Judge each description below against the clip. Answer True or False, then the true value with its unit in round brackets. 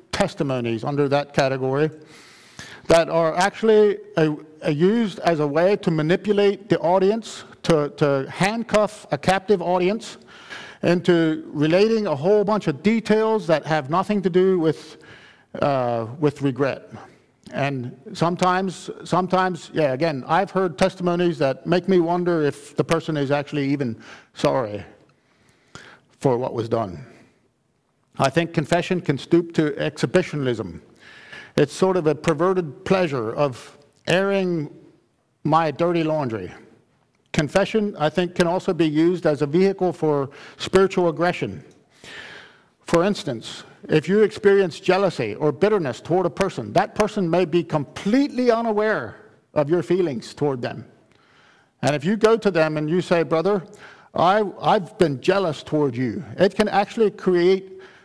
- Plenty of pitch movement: False (4.2 semitones)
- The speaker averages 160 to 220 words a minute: False (140 wpm)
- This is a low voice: False (170 Hz)